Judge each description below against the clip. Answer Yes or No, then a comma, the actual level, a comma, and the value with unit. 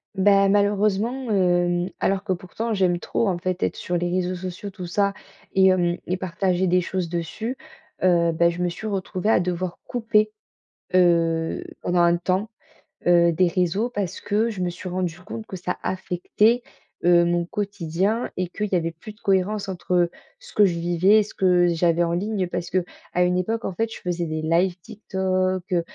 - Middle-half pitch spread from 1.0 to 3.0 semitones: Yes, narrow, 2.5 semitones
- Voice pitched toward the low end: No, medium, 185 Hz